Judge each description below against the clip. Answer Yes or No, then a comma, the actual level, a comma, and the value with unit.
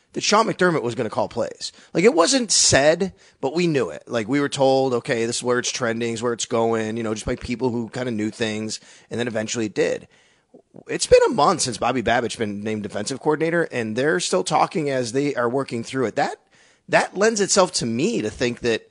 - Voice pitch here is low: Yes, low, 120 Hz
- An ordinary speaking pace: No, fast, 240 wpm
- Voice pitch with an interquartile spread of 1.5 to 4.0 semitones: No, average, 4.7 semitones